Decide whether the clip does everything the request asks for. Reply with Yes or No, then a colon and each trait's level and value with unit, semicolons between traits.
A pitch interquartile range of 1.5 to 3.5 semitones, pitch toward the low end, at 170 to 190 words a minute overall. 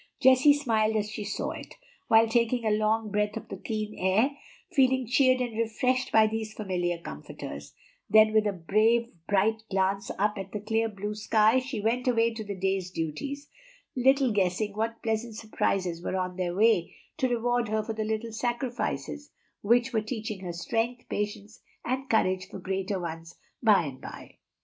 No: average, 3.2 semitones; high, 215 Hz; average, 175 wpm